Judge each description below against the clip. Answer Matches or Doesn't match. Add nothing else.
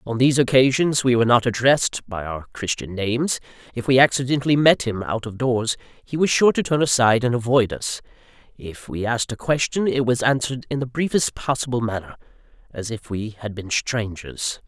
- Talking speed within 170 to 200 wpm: Matches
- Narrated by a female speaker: Doesn't match